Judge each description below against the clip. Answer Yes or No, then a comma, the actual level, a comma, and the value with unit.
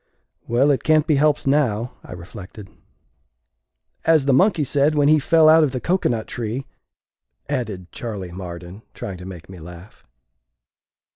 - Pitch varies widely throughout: Yes, wide, 7.8 semitones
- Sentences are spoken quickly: No, average, 155 wpm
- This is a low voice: Yes, low, 120 Hz